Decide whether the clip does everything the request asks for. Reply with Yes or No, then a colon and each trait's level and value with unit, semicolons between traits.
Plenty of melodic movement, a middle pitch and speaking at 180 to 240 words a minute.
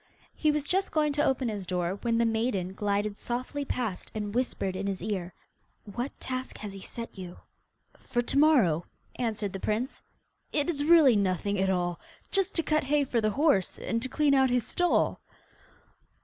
No: wide, 6.1 semitones; high, 230 Hz; average, 185 wpm